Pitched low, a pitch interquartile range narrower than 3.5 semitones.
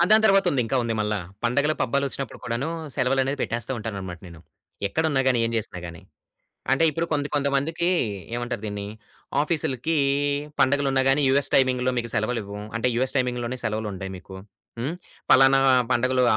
No: low, 130 Hz; average, 3.8 semitones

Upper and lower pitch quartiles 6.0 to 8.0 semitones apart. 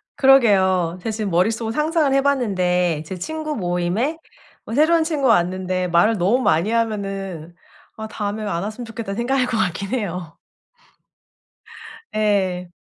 No: average, 5.3 semitones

